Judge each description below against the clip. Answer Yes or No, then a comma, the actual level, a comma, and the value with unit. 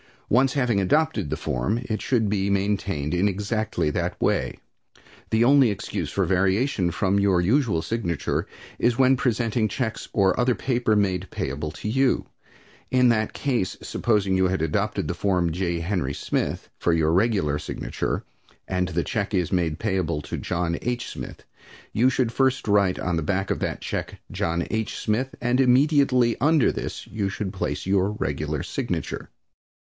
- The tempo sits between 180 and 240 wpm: No, average, 165 wpm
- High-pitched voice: No, low, 100 Hz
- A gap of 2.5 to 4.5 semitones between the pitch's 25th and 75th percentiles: No, average, 4.9 semitones